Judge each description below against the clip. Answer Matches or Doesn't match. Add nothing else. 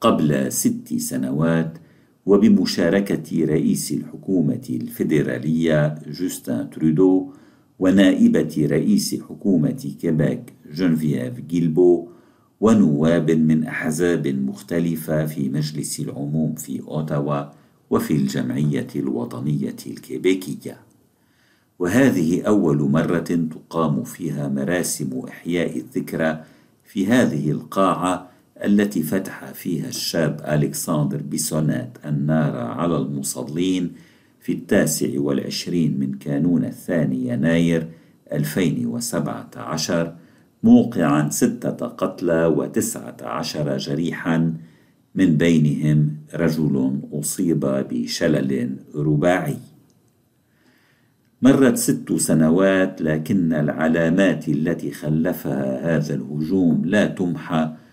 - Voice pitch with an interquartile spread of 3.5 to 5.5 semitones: Doesn't match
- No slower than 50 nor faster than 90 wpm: Matches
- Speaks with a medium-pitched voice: Doesn't match